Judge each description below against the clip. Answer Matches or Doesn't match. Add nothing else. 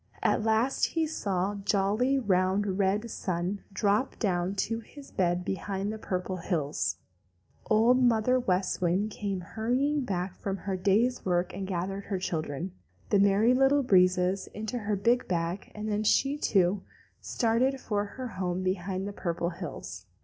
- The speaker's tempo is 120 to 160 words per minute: Matches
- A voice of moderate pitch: Doesn't match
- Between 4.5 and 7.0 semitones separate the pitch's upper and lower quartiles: Doesn't match